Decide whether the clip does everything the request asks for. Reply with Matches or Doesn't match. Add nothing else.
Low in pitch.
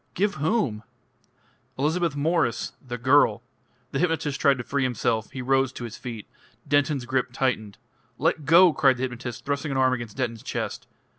Matches